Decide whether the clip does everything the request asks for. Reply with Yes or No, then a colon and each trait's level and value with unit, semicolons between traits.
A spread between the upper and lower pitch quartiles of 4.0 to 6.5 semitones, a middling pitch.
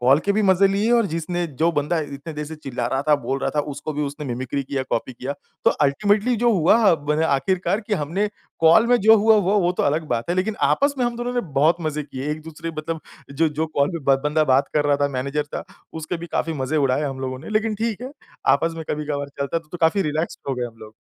Yes: average, 5.1 semitones; medium, 155 Hz